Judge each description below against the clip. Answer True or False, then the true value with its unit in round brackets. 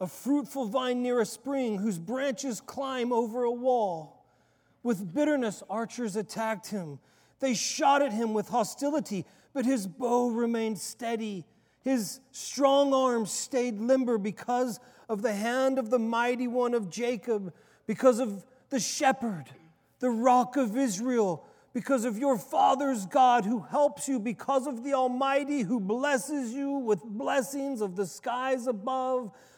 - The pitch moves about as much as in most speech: True (3.1 semitones)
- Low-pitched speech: False (245 Hz)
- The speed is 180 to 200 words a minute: False (145 wpm)